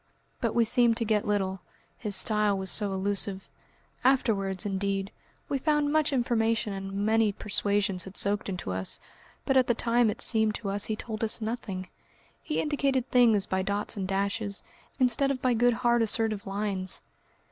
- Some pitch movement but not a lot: Yes, average, 3.4 semitones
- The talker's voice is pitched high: Yes, high, 215 Hz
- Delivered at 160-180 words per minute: Yes, average, 170 wpm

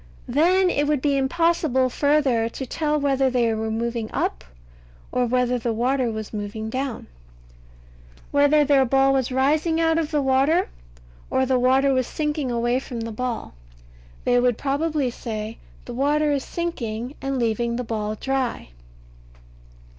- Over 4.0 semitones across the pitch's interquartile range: No, average, 3.5 semitones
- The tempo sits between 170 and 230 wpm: No, average, 155 wpm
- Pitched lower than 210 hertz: No, very high, 260 Hz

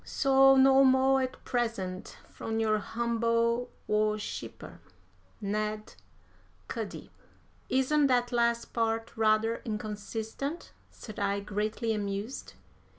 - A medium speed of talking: No, slow, 95 wpm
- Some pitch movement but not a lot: Yes, average, 3.1 semitones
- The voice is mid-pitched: No, high, 225 Hz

